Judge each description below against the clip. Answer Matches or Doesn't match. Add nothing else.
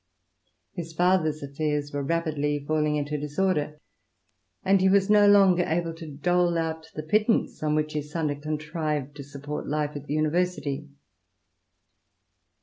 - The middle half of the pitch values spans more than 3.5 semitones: Doesn't match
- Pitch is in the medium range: Matches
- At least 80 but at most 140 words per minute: Doesn't match